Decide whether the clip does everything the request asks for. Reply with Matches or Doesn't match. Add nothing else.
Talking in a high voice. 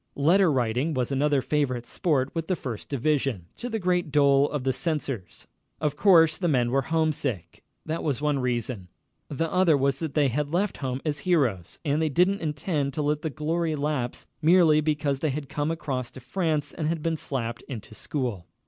Doesn't match